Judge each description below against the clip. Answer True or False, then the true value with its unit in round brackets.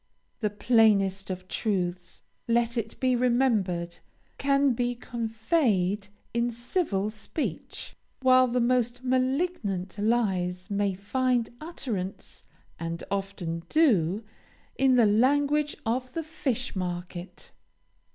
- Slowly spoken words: True (105 wpm)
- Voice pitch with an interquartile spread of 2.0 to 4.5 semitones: False (4.9 semitones)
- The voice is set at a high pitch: True (225 Hz)